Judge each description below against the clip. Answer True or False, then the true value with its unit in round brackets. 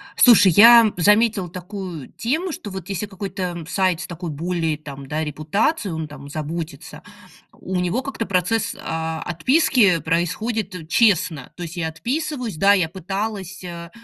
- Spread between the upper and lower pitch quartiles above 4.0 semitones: True (4.5 semitones)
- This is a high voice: False (180 Hz)